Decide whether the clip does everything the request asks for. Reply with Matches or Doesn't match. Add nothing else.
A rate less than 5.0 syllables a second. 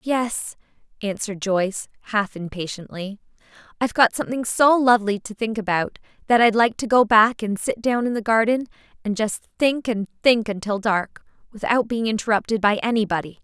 Doesn't match